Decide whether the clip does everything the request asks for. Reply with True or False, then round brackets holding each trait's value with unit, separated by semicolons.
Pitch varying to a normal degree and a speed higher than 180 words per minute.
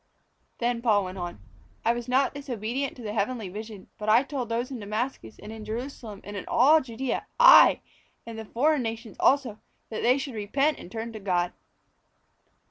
True (3.4 semitones; 190 wpm)